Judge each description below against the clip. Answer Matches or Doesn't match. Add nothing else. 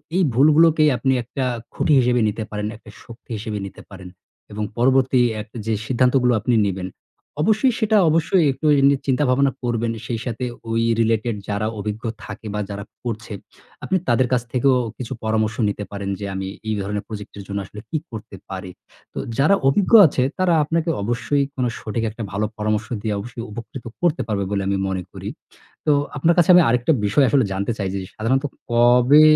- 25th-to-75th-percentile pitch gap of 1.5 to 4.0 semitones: Doesn't match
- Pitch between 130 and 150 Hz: Doesn't match